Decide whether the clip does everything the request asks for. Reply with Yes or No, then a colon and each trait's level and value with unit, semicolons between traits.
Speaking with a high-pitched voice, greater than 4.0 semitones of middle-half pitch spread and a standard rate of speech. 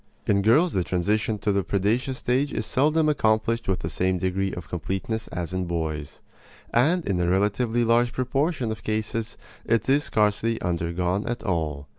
No: low, 105 Hz; average, 4.6 semitones; average, 170 wpm